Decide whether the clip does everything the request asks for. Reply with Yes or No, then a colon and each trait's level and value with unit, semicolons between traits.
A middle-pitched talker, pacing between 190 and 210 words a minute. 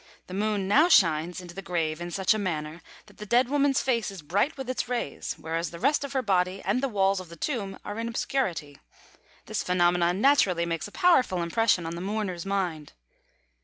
No: high, 195 Hz; fast, 205 wpm